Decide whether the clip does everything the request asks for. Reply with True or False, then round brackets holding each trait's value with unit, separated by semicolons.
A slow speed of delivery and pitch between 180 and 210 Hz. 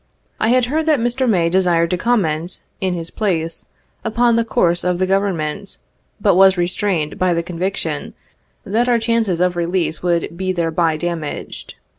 False (165 wpm; 185 Hz)